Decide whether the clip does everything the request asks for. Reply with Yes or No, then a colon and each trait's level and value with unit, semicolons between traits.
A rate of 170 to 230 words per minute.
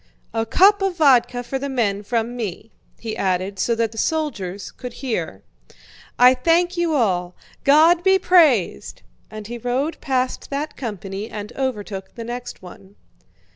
No: average, 155 wpm